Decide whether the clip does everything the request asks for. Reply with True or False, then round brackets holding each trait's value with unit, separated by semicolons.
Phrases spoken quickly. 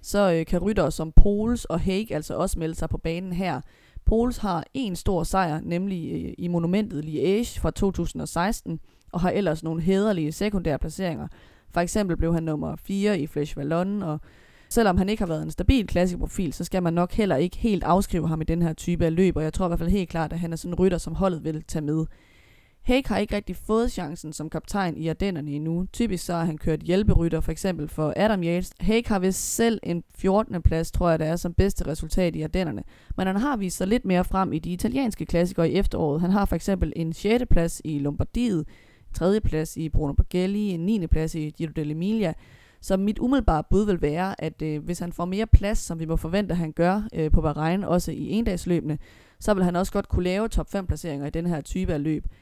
True (230 wpm)